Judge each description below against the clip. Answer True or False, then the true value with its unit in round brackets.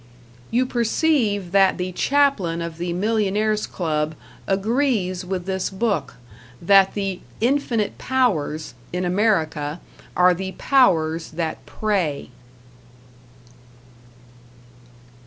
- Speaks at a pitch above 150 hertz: True (190 Hz)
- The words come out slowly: True (95 wpm)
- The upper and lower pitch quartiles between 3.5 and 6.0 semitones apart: True (4.3 semitones)